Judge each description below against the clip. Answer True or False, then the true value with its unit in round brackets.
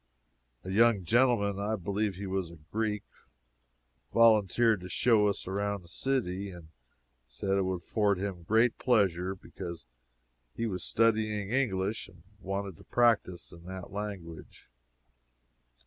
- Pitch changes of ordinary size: True (3.0 semitones)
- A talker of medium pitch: False (100 Hz)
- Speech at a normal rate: False (130 wpm)